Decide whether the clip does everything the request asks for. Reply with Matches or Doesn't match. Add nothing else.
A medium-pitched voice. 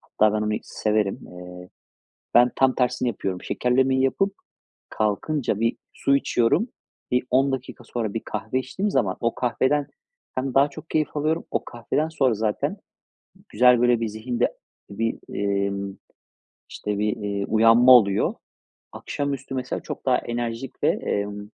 Doesn't match